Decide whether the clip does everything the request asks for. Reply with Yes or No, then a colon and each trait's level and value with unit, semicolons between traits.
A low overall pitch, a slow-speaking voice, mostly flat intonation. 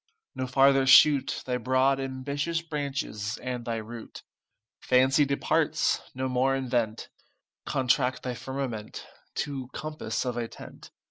Yes: low, 130 Hz; slow, 125 wpm; narrow, 1.8 semitones